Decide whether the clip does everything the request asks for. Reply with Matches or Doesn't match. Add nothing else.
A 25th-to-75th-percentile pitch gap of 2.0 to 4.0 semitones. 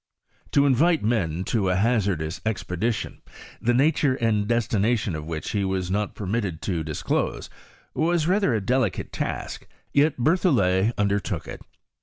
Doesn't match